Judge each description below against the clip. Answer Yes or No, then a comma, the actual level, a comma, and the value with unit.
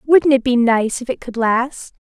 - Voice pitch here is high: Yes, very high, 250 Hz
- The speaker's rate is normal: No, fast, 225 wpm